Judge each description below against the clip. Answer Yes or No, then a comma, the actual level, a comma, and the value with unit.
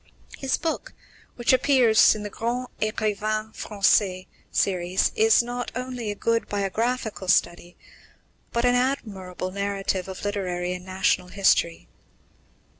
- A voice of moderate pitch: No, high, 210 Hz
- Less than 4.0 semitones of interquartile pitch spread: No, average, 4.4 semitones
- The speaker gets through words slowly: Yes, slow, 120 wpm